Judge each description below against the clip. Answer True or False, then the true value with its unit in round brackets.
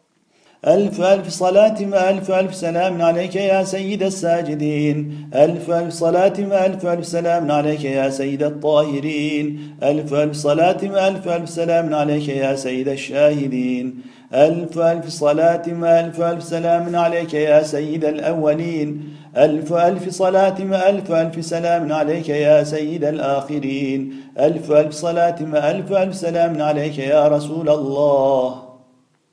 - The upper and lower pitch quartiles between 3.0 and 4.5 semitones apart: False (2.5 semitones)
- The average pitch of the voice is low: False (155 Hz)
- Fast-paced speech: False (125 wpm)